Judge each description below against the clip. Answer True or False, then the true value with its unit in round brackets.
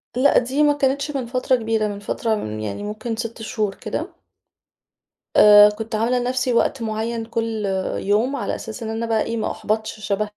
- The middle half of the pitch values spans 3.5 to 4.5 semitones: False (2.5 semitones)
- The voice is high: True (225 Hz)